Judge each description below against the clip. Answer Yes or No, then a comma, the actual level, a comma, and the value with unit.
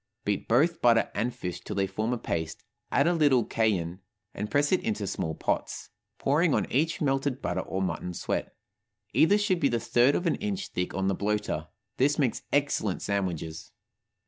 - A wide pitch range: Yes, wide, 7.0 semitones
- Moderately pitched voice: No, low, 115 Hz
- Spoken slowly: No, average, 185 wpm